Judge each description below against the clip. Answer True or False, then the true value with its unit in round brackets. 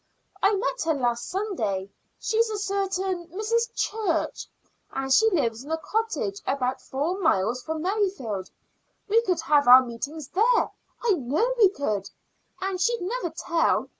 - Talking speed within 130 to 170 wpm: True (150 wpm)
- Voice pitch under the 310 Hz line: False (345 Hz)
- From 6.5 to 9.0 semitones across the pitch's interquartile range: True (7.8 semitones)